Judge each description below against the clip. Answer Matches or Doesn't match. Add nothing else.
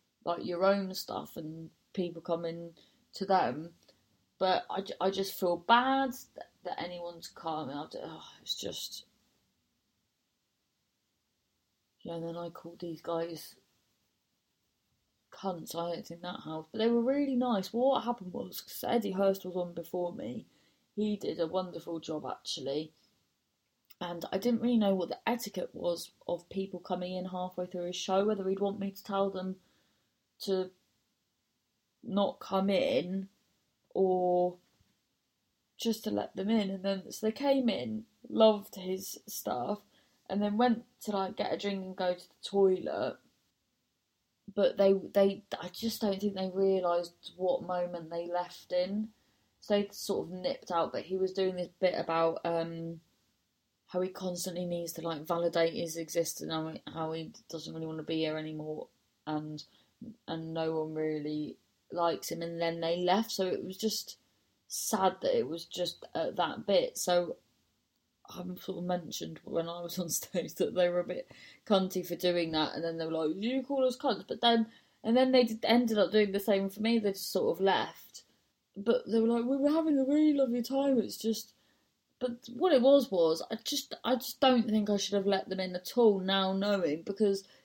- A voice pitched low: Doesn't match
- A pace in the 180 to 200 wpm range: Matches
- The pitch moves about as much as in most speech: Matches